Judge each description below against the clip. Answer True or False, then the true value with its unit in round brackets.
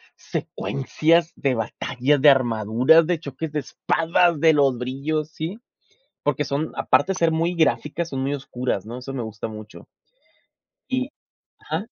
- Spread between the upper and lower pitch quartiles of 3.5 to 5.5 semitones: True (4.2 semitones)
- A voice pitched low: False (145 Hz)